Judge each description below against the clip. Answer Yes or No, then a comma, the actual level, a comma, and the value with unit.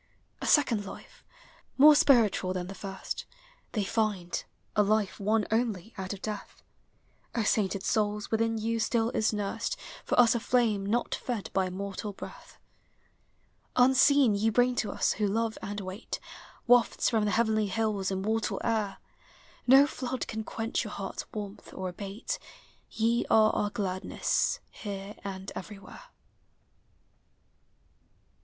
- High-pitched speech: Yes, high, 215 Hz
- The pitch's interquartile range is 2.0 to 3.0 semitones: Yes, narrow, 2.5 semitones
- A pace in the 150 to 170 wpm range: No, average, 140 wpm